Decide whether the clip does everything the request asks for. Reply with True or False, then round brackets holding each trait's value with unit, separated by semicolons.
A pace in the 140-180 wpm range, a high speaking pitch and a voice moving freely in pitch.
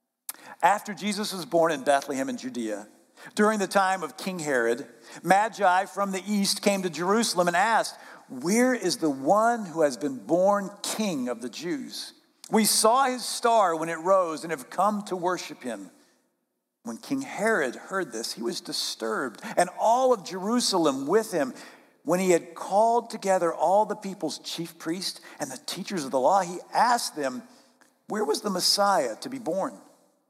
True (175 wpm; 200 Hz; 6.0 semitones)